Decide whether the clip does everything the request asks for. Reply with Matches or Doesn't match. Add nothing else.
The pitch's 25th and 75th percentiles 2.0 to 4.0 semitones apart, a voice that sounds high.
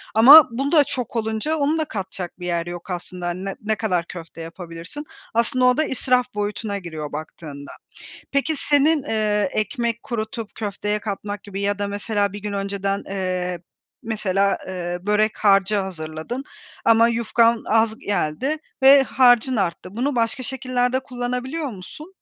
Doesn't match